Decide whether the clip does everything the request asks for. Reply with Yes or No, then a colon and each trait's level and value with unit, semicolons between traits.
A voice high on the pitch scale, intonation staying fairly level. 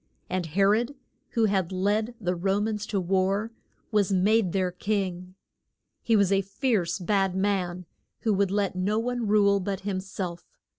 Yes: high, 195 Hz; narrow, 2.2 semitones